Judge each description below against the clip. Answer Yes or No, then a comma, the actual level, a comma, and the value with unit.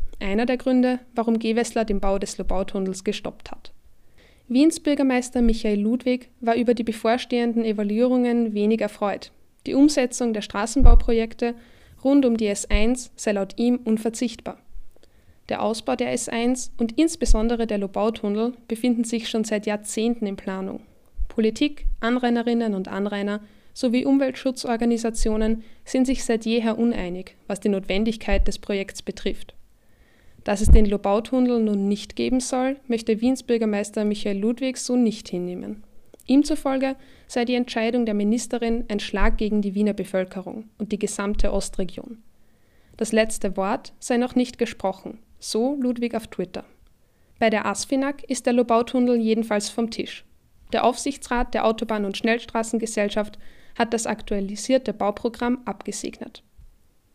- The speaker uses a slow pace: No, average, 135 wpm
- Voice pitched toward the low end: No, high, 230 Hz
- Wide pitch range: No, average, 2.8 semitones